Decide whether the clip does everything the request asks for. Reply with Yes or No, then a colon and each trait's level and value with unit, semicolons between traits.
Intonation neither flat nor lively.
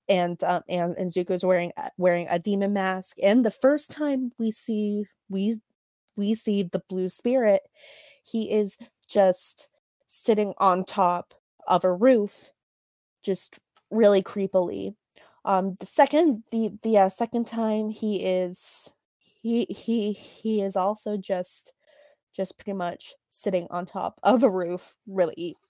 Yes: average, 3.6 semitones